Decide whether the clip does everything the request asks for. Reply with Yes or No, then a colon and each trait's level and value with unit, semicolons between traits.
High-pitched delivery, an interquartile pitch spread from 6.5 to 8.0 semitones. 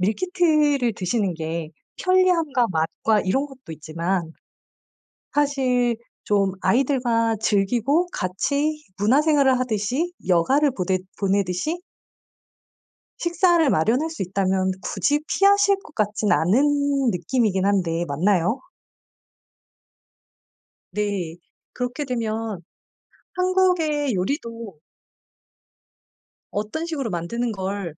Yes: high, 230 Hz; wide, 7.3 semitones